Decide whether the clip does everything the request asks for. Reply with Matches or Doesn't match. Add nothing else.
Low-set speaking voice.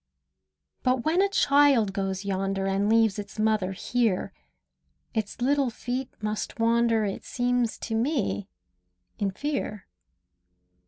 Doesn't match